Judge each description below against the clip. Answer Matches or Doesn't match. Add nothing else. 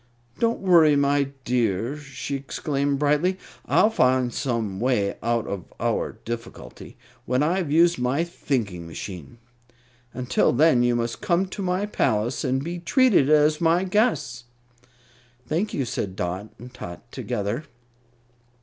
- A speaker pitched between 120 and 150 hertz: Matches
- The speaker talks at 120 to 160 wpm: Matches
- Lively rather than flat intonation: Matches